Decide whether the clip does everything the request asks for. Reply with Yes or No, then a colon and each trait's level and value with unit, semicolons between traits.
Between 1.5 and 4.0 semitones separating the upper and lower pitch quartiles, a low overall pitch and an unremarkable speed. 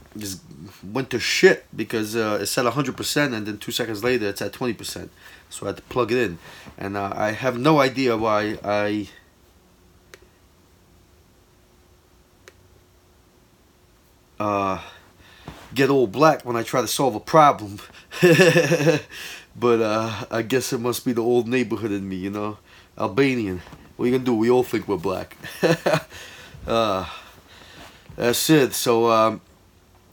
No: average, 4.8 semitones; low, 110 Hz; average, 150 wpm